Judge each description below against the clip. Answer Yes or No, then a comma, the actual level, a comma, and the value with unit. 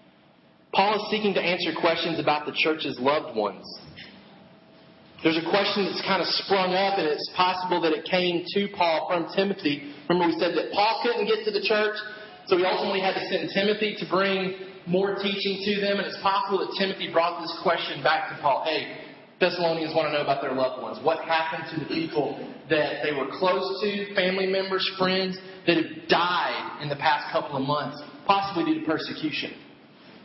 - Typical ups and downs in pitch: Yes, average, 3.5 semitones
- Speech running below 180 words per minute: No, average, 195 wpm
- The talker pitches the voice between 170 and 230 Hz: Yes, medium, 185 Hz